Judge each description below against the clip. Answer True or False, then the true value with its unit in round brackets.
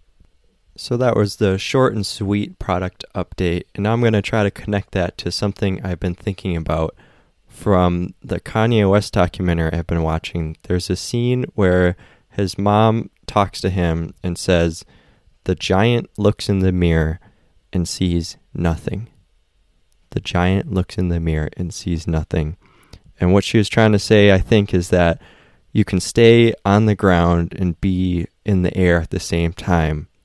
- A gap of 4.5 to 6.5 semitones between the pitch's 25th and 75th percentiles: False (3.2 semitones)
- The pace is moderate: True (175 wpm)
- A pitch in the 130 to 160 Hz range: False (95 Hz)